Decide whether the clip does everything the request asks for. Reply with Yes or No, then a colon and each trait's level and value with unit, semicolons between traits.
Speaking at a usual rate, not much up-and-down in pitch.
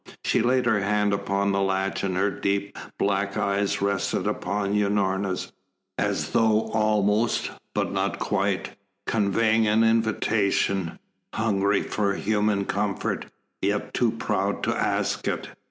No: slow, 130 wpm; narrow, 1.6 semitones